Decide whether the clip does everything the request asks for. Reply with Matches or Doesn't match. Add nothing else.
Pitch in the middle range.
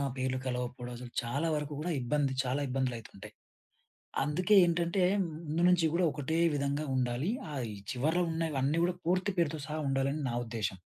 Matches